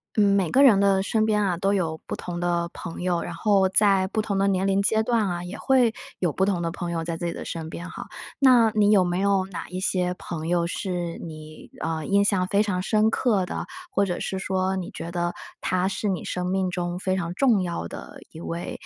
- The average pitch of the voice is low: No, medium, 185 Hz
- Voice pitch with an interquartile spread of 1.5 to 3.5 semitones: Yes, narrow, 2.5 semitones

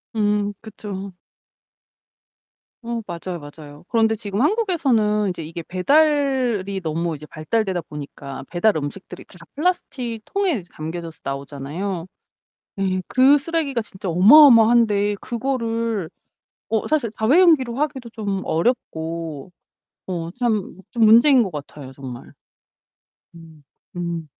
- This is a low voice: No, high, 205 Hz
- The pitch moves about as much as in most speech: No, wide, 6.3 semitones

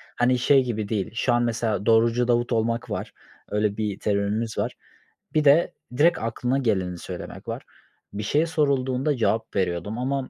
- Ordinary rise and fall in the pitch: Yes, average, 3.5 semitones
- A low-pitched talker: Yes, low, 115 Hz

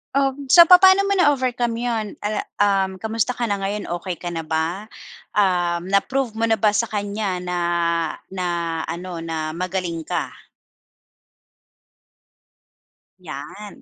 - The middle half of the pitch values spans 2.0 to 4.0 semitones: No, average, 4.8 semitones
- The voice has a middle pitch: No, high, 205 Hz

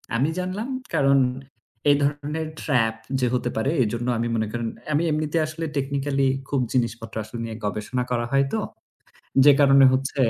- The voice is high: No, low, 135 Hz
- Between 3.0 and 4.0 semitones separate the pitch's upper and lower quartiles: Yes, average, 3.7 semitones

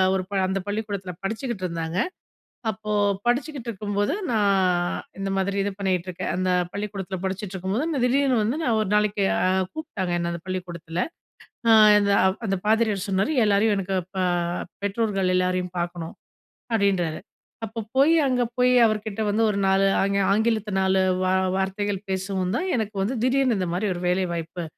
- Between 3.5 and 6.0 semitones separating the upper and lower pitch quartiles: No, average, 2.9 semitones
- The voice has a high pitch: Yes, high, 200 Hz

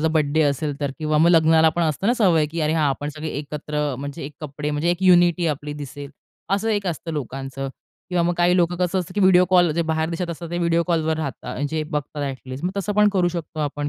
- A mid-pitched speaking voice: Yes, medium, 160 Hz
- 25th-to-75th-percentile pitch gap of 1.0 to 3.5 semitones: Yes, average, 3.0 semitones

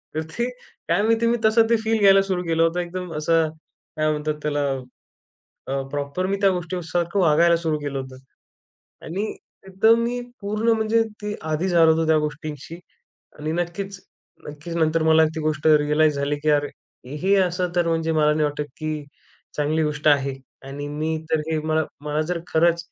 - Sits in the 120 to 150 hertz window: No, medium, 160 Hz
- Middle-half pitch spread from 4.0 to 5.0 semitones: No, average, 3.4 semitones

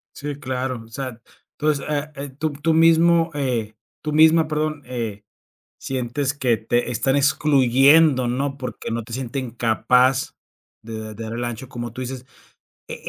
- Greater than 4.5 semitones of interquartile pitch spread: No, average, 3.5 semitones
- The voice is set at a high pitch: No, low, 130 Hz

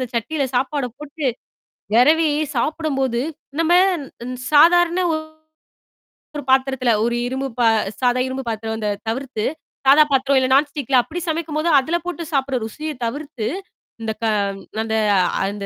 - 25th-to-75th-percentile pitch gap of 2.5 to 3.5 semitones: No, average, 4.2 semitones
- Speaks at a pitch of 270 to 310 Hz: Yes, very high, 275 Hz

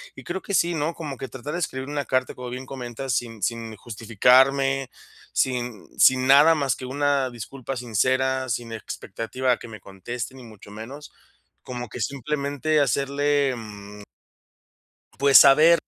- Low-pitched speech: Yes, low, 130 Hz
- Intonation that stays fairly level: No, average, 3.0 semitones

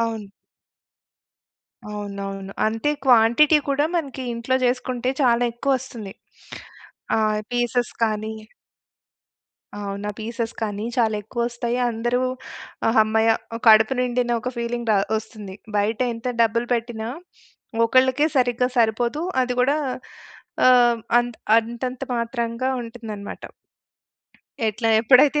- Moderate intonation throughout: No, narrow, 2.2 semitones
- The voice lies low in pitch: No, high, 235 Hz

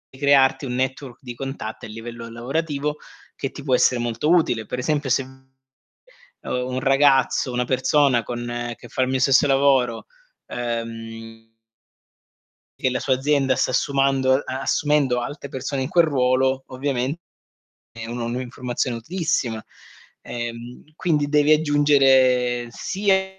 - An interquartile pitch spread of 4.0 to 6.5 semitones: No, average, 2.8 semitones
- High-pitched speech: No, low, 130 Hz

